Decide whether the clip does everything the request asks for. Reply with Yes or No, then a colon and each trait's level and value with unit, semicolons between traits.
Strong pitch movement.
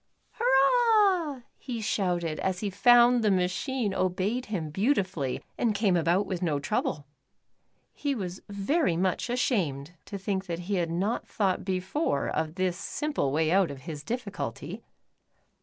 Yes: wide, 5.7 semitones